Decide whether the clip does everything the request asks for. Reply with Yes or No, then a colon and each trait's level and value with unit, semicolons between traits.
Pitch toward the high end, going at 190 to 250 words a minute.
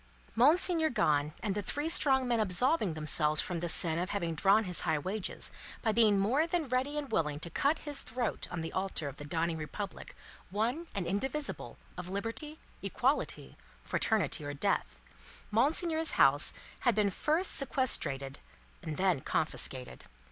No: high, 205 Hz; average, 160 wpm